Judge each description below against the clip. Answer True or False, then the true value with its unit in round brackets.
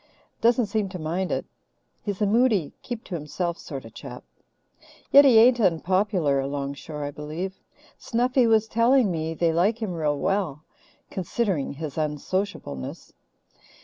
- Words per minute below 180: True (145 wpm)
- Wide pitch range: True (6.5 semitones)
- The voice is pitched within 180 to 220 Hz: True (185 Hz)